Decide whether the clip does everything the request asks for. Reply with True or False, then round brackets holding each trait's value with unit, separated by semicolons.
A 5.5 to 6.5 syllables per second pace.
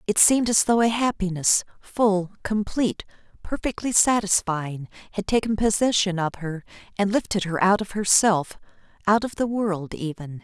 False (4.9 syllables/s)